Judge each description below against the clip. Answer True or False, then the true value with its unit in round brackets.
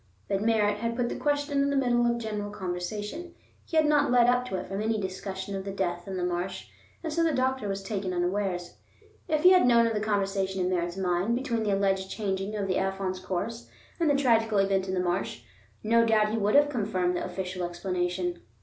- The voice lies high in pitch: True (200 Hz)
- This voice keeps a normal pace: False (220 wpm)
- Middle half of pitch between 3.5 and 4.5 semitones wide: True (4.0 semitones)